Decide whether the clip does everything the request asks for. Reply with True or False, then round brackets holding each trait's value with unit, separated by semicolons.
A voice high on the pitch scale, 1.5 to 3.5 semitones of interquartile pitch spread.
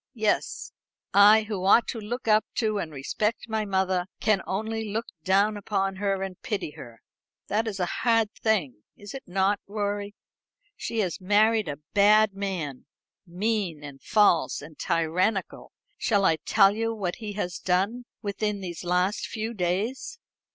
True (205 Hz; 2.8 semitones)